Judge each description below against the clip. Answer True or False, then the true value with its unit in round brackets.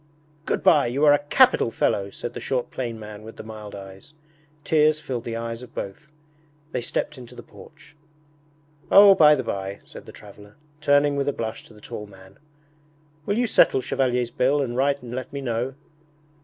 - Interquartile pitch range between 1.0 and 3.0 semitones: False (4.7 semitones)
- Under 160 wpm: False (195 wpm)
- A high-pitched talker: False (125 Hz)